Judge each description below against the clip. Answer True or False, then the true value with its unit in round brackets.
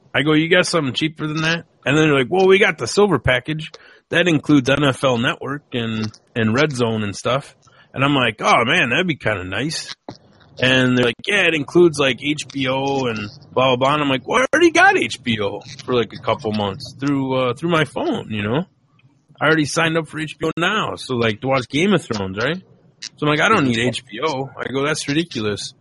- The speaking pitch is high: False (140 Hz)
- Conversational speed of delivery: False (225 wpm)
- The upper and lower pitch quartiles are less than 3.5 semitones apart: False (4.1 semitones)